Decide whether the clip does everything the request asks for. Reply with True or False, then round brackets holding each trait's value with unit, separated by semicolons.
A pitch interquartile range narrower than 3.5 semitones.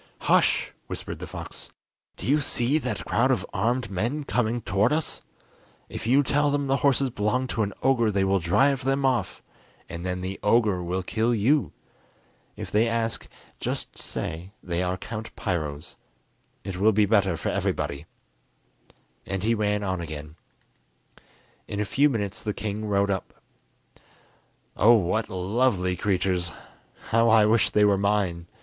False (4.2 semitones)